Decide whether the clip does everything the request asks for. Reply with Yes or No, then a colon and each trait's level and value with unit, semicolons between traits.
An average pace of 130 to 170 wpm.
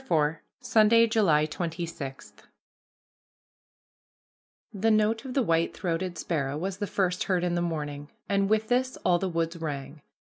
Yes: average, 145 wpm